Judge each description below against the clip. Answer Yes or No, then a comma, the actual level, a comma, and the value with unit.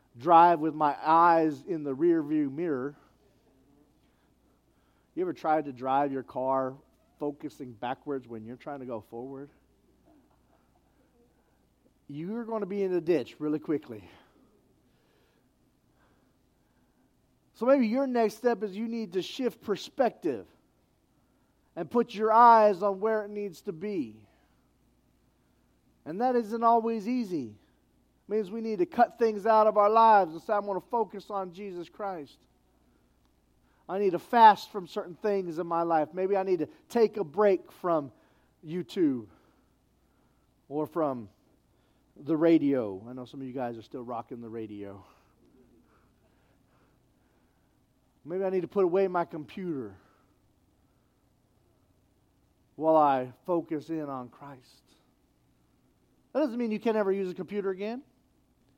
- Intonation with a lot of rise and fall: Yes, wide, 8.2 semitones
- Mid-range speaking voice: Yes, medium, 170 Hz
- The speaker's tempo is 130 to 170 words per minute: Yes, average, 140 wpm